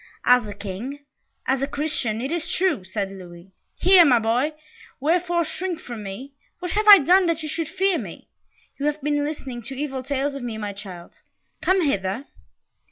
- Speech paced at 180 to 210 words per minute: Yes, average, 185 wpm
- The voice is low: No, very high, 275 Hz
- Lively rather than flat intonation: Yes, wide, 7.0 semitones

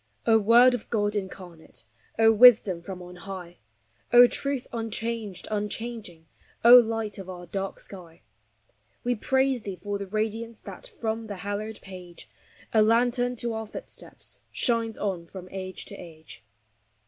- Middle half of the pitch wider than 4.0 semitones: No, average, 3.6 semitones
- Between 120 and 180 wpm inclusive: Yes, average, 150 wpm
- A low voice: No, high, 215 Hz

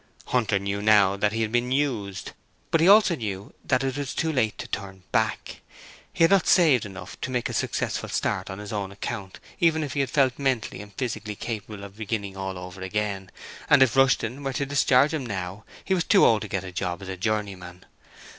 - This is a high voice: No, low, 110 Hz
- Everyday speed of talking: No, fast, 220 wpm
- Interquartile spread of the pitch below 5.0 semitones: No, wide, 5.4 semitones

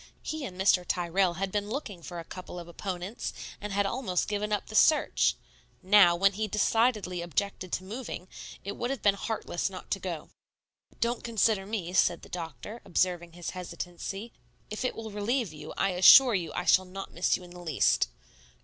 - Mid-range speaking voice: No, high, 195 Hz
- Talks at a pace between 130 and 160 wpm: No, average, 190 wpm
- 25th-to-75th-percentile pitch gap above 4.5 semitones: No, average, 3.2 semitones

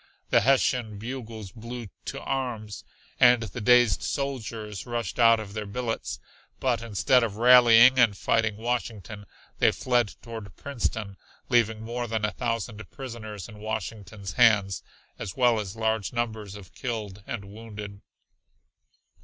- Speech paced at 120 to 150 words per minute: Yes, slow, 135 wpm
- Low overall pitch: Yes, low, 110 Hz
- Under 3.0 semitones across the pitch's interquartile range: Yes, narrow, 2.4 semitones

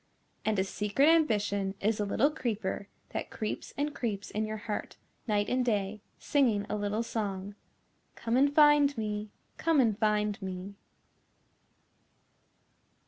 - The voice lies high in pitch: Yes, high, 215 Hz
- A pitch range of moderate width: Yes, average, 3.7 semitones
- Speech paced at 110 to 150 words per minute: Yes, average, 140 wpm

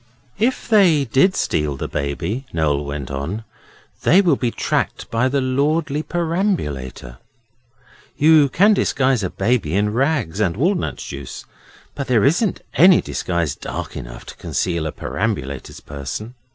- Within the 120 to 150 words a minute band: Yes, average, 140 wpm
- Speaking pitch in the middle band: No, low, 115 Hz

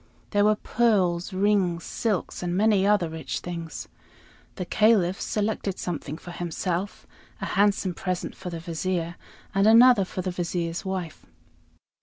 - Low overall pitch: No, medium, 185 Hz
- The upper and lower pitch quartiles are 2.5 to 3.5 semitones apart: Yes, average, 3.0 semitones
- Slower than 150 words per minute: Yes, average, 140 wpm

